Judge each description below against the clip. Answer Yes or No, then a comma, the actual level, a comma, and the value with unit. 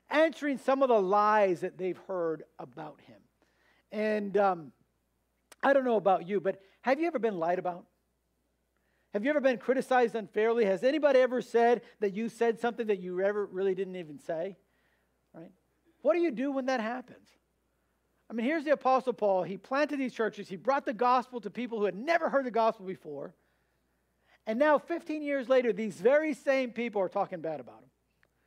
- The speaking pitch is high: Yes, high, 220 Hz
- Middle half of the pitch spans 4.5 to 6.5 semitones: Yes, wide, 5.6 semitones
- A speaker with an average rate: Yes, average, 190 wpm